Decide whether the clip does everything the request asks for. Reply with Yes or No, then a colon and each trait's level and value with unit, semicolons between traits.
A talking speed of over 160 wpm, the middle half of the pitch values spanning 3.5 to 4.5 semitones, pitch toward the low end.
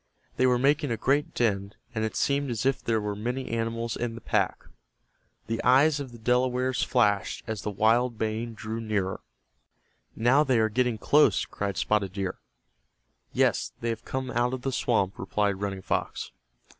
No: average, 175 wpm; average, 3.0 semitones; low, 115 Hz